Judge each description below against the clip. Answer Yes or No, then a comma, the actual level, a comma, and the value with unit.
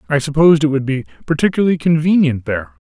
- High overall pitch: No, medium, 145 Hz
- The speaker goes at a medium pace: Yes, average, 165 wpm